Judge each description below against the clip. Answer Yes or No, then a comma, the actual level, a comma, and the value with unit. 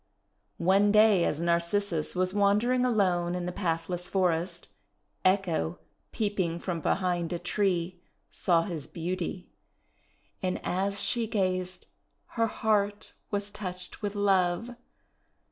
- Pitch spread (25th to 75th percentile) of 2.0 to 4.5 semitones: Yes, narrow, 2.6 semitones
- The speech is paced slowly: Yes, slow, 115 wpm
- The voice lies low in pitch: No, medium, 185 Hz